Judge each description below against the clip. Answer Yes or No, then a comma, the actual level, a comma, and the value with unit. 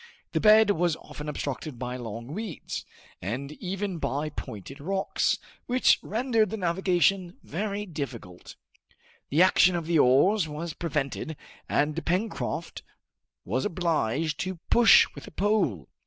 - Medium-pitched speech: Yes, medium, 165 Hz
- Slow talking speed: Yes, slow, 130 wpm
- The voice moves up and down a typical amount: No, wide, 5.8 semitones